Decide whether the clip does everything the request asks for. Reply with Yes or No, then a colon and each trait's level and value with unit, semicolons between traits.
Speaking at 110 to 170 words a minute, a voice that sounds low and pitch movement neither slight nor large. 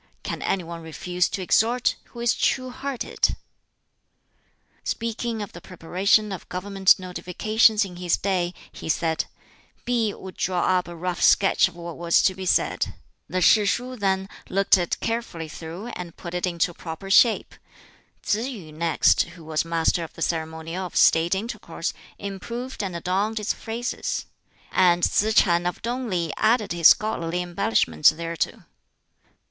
No: average, 155 wpm; medium, 185 Hz; average, 4.0 semitones